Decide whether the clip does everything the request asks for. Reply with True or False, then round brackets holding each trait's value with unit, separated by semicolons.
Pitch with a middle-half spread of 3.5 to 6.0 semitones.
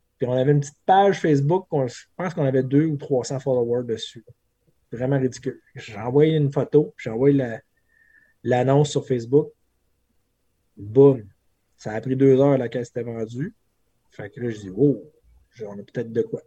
True (3.8 semitones)